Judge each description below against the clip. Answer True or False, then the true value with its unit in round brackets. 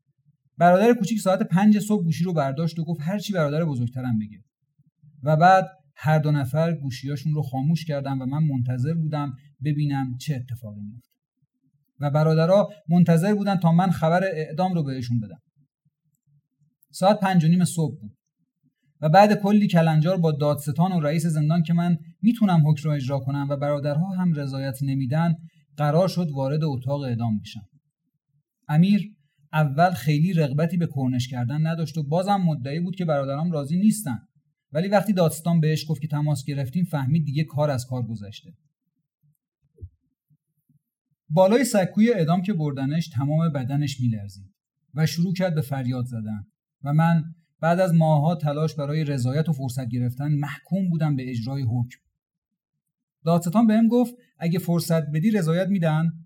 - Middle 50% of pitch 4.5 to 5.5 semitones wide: False (3.4 semitones)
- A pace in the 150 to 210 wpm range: True (155 wpm)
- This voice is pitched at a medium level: True (155 Hz)